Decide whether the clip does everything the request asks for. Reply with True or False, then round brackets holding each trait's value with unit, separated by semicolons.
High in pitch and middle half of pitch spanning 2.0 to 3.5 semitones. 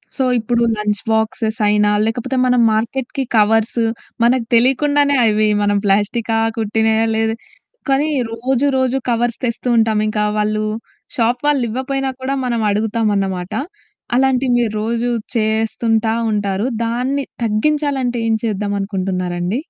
True (225 Hz; 3.0 semitones)